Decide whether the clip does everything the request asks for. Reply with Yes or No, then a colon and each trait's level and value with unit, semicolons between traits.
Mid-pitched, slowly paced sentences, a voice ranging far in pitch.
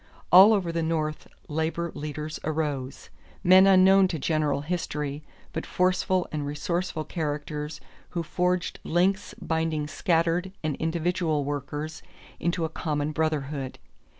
No: medium, 160 Hz; slow, 125 wpm; average, 2.9 semitones